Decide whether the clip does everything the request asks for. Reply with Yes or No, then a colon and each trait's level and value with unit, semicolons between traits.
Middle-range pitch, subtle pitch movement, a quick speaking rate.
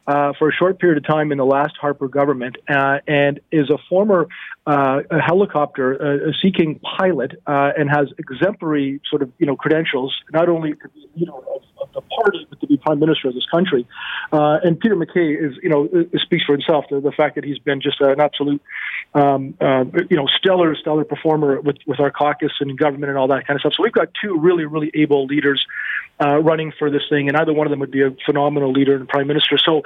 Yes: medium, 150 Hz; narrow, 2.0 semitones; fast, 230 wpm